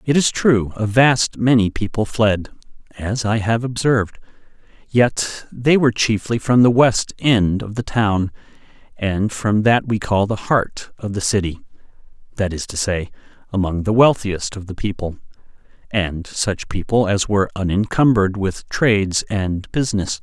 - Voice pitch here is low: Yes, low, 105 Hz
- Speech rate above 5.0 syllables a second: No, 4.4 syllables/s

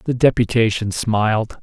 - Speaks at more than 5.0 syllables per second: No, 4.4 syllables/s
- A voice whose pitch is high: No, low, 115 Hz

